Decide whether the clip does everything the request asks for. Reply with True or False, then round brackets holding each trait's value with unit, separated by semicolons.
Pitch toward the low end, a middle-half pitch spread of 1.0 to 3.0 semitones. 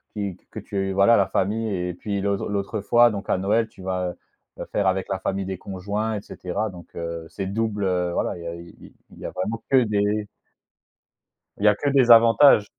True (100 Hz; 2.5 semitones)